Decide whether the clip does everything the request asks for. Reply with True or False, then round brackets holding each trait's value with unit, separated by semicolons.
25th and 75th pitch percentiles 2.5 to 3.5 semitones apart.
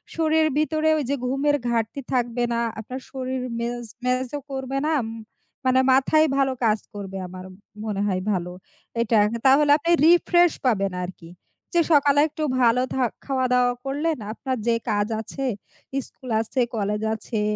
False (4.4 semitones)